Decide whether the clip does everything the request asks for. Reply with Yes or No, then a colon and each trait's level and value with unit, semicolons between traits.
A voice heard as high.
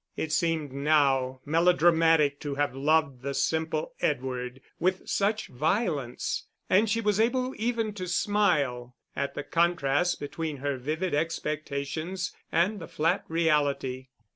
No: medium, 155 Hz